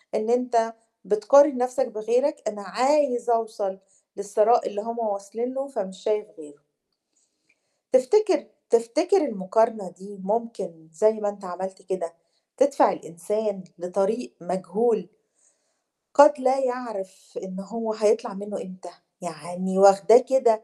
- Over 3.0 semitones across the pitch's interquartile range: Yes, average, 4.1 semitones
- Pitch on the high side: Yes, high, 215 Hz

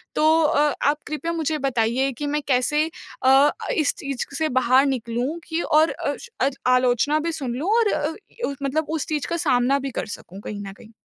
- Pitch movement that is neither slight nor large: Yes, average, 3.4 semitones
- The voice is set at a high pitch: Yes, very high, 280 Hz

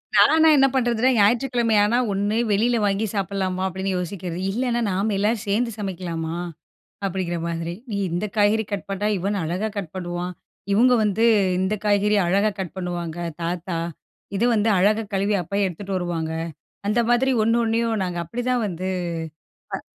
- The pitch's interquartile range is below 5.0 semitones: Yes, average, 3.7 semitones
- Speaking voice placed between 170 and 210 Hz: Yes, high, 200 Hz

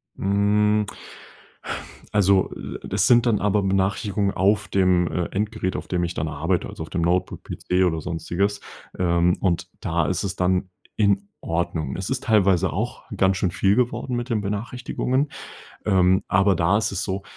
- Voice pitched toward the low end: Yes, very low, 95 Hz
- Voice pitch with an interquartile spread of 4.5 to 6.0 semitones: No, average, 2.7 semitones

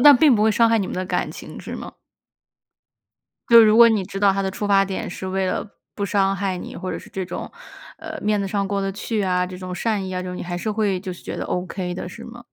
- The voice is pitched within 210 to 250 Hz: No, high, 195 Hz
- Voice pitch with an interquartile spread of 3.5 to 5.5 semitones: No, average, 2.7 semitones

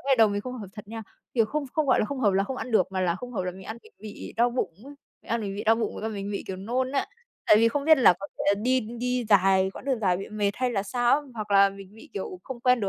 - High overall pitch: Yes, high, 220 Hz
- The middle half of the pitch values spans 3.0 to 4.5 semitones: Yes, average, 4.1 semitones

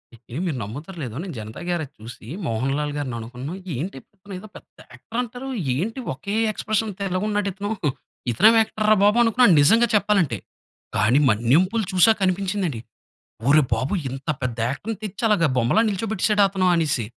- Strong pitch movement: Yes, wide, 8.0 semitones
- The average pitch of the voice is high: No, medium, 180 Hz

